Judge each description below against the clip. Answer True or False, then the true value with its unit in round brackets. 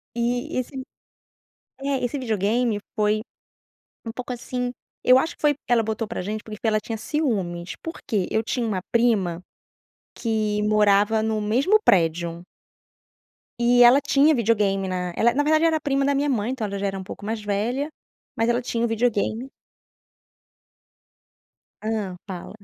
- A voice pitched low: False (225 Hz)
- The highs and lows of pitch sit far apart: False (3.4 semitones)